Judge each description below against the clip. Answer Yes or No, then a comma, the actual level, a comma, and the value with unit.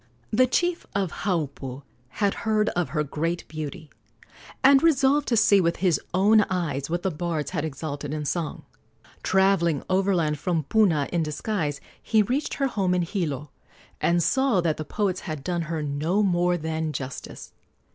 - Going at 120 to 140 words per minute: No, average, 165 wpm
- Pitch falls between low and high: Yes, medium, 175 Hz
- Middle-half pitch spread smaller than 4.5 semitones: No, average, 4.8 semitones